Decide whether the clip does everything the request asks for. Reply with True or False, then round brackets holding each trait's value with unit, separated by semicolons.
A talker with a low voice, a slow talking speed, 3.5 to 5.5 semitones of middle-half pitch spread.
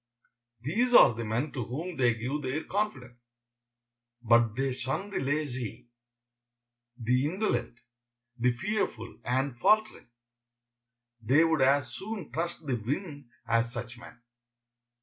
True (130 Hz; 130 wpm; 4.7 semitones)